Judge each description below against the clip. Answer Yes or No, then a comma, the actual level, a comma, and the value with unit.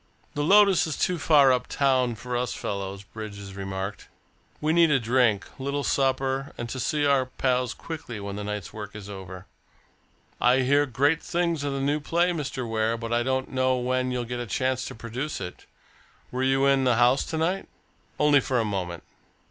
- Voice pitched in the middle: No, low, 130 Hz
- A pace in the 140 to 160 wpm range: No, average, 195 wpm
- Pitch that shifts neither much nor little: Yes, average, 4.2 semitones